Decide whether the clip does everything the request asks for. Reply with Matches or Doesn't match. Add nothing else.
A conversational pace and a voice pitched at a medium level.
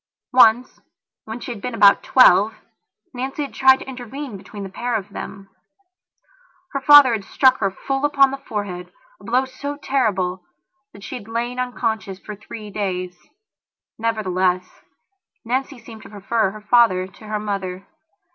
Doesn't match